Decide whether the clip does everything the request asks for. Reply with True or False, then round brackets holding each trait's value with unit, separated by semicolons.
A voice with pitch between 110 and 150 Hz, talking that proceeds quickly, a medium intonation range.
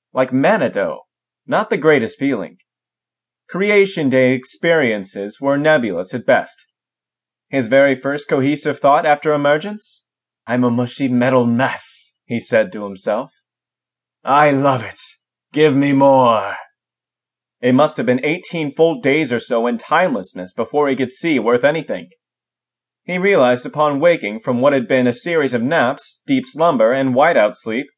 False (140 Hz; 150 wpm; 3.7 semitones)